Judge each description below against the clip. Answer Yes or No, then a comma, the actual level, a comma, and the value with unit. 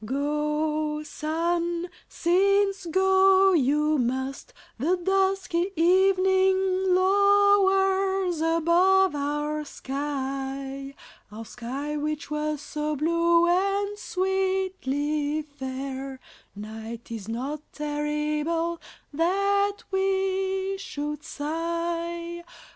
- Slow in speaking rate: Yes, slow, 80 wpm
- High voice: Yes, very high, 335 Hz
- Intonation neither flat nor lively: Yes, average, 4.6 semitones